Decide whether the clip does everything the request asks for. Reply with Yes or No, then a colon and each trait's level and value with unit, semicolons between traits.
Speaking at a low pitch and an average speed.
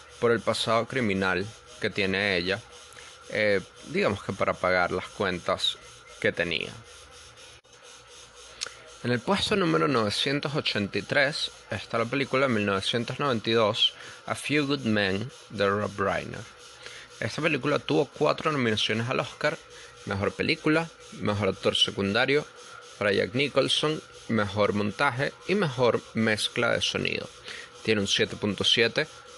No: low, 120 Hz; slow, 120 wpm